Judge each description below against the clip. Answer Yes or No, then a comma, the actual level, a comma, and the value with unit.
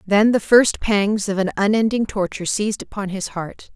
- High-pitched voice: Yes, high, 205 Hz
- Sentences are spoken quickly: No, average, 190 wpm